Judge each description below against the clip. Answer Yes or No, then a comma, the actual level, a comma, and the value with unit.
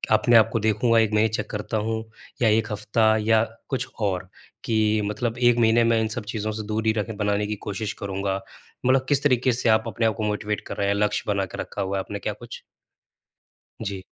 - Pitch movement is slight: Yes, narrow, 1.8 semitones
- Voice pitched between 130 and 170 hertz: No, low, 110 Hz